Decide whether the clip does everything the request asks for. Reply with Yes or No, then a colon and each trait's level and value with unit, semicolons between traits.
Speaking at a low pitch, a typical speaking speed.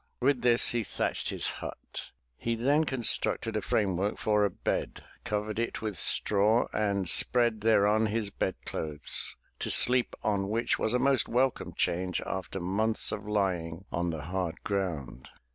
Yes: low, 105 Hz; average, 160 wpm